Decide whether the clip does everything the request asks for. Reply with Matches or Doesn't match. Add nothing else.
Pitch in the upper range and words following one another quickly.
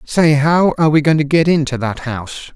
Doesn't match